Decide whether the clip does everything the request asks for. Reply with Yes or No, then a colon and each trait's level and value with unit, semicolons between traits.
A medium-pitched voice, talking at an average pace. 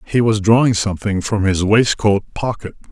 No: low, 105 Hz; average, 165 wpm